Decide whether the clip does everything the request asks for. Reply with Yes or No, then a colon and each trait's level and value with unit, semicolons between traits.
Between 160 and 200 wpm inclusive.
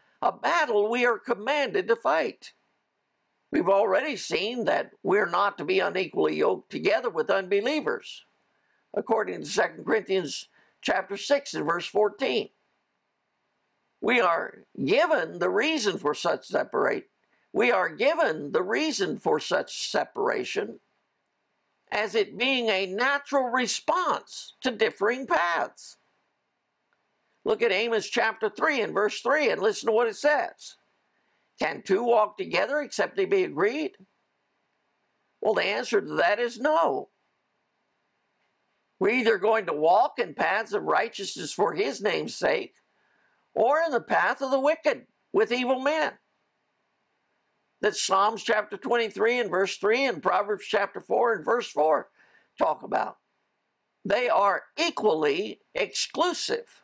No: slow, 135 wpm